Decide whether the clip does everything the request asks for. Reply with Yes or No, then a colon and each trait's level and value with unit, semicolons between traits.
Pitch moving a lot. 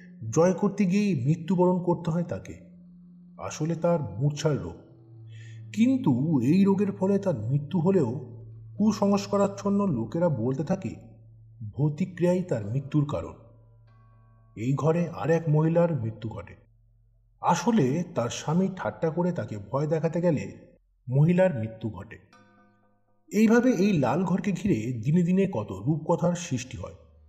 Yes: wide, 8.1 semitones